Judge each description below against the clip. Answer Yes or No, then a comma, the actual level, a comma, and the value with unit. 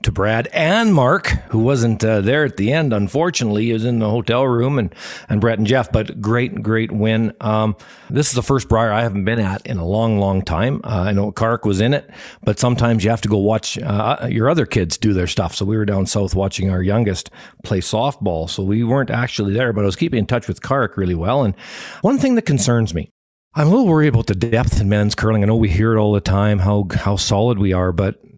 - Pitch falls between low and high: No, low, 110 Hz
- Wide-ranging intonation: No, average, 2.9 semitones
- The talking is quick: Yes, fast, 245 wpm